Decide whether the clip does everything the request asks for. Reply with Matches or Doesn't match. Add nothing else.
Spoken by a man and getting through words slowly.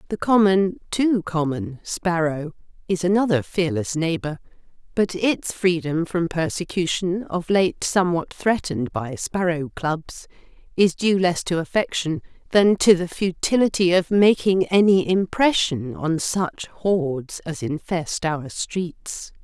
Doesn't match